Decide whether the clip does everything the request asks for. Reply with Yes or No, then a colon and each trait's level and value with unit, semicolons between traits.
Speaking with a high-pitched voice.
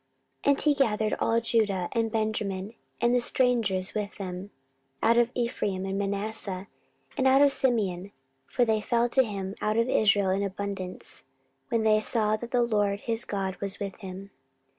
Yes: high, 215 Hz